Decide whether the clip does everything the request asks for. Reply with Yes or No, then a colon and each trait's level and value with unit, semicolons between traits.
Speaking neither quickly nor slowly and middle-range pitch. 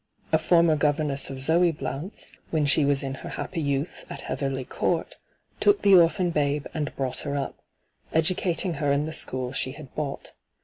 Yes: average, 180 wpm; medium, 150 Hz